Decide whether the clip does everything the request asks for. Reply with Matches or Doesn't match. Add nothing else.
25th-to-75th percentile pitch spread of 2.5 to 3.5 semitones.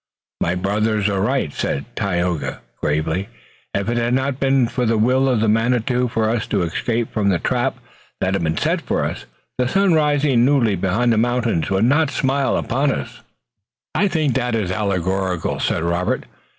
Doesn't match